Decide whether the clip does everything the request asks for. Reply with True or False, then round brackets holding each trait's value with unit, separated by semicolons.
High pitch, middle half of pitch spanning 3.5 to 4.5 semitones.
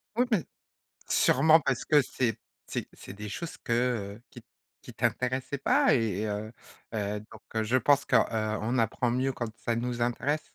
False (120 Hz; 3.9 semitones)